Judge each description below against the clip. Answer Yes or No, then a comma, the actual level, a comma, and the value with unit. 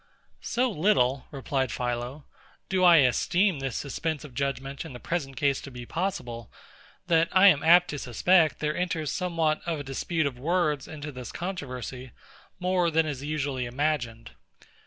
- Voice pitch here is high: No, medium, 145 Hz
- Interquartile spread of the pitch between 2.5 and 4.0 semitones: No, average, 4.6 semitones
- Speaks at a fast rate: No, average, 160 wpm